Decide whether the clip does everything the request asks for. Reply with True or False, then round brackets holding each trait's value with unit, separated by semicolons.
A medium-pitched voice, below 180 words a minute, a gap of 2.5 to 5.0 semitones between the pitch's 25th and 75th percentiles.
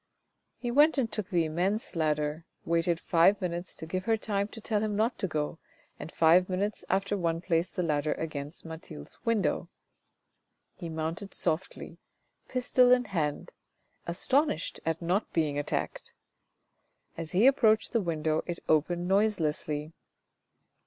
True (175 Hz; 145 wpm; 4.4 semitones)